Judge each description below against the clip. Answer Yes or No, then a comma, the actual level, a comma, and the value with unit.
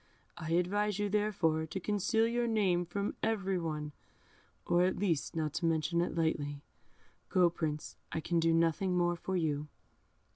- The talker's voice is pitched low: No, medium, 175 Hz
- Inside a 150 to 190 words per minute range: Yes, average, 160 wpm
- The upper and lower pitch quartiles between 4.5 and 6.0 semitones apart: No, average, 3.8 semitones